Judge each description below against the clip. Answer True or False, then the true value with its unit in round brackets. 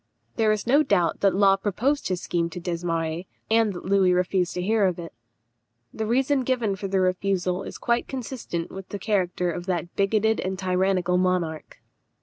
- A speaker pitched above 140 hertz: True (190 Hz)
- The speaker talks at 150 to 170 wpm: False (180 wpm)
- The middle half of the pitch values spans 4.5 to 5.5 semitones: False (3.1 semitones)